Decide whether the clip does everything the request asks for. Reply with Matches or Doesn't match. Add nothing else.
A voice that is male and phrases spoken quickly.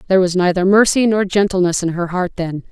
Doesn't match